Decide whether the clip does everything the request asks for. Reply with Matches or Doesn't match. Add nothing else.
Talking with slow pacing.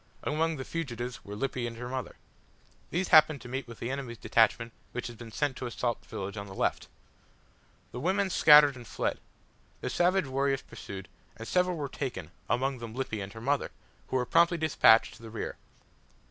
Doesn't match